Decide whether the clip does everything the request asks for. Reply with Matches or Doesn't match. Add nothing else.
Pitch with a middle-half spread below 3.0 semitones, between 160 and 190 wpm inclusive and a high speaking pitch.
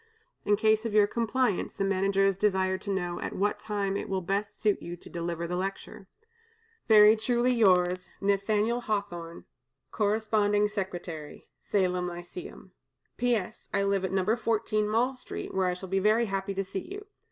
Matches